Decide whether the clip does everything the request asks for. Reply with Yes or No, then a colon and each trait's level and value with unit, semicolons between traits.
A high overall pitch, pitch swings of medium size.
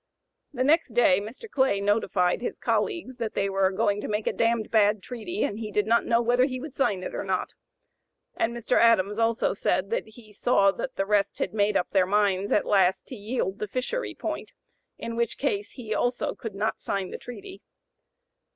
Yes: high, 220 Hz; average, 3.5 semitones